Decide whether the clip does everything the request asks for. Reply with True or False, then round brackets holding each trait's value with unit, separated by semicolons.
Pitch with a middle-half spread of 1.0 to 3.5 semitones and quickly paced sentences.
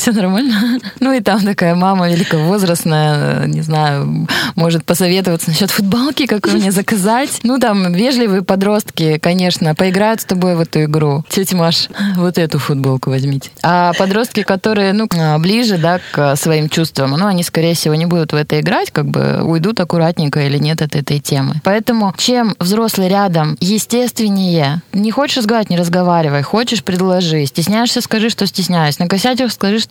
False (5.0 semitones; 165 wpm)